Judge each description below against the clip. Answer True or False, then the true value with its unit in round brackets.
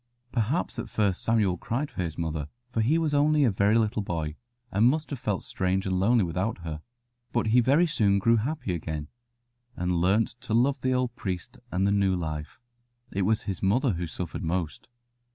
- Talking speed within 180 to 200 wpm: True (195 wpm)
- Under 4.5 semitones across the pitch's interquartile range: False (5.1 semitones)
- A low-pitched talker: True (100 Hz)